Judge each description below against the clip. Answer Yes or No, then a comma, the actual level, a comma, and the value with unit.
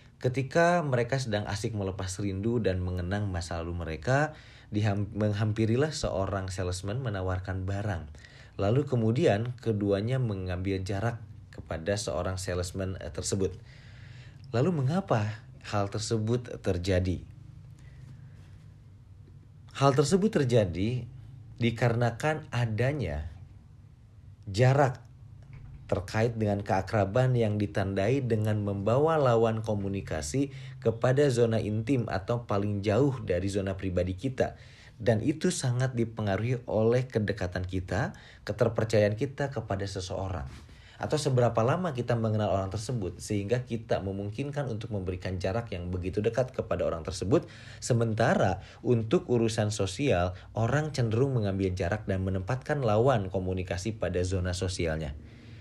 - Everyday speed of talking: Yes, average, 110 wpm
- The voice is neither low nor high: No, low, 110 Hz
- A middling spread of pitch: Yes, average, 4.1 semitones